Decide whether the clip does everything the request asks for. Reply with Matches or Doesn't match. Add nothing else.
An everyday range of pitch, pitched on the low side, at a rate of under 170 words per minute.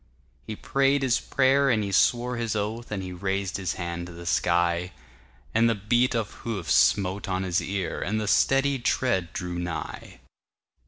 Matches